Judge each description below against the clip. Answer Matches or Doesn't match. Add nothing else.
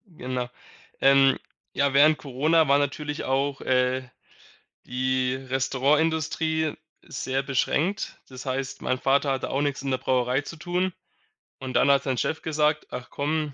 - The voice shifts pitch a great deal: Doesn't match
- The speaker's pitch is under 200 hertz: Matches